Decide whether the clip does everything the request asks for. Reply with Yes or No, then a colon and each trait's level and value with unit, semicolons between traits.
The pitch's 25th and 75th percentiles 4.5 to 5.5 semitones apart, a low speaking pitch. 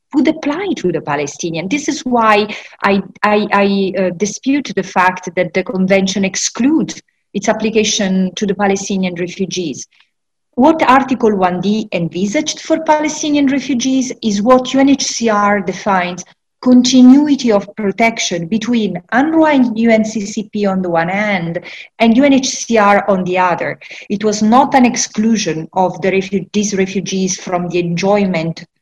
No: average, 5.0 semitones; high, 205 Hz